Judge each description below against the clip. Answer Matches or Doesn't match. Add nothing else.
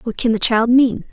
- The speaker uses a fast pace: Matches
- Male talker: Doesn't match